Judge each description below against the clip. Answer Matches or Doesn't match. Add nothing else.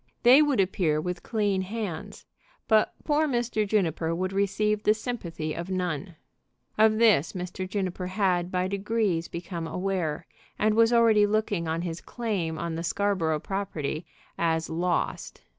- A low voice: Doesn't match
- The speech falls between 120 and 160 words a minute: Matches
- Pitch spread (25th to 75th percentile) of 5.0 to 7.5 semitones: Doesn't match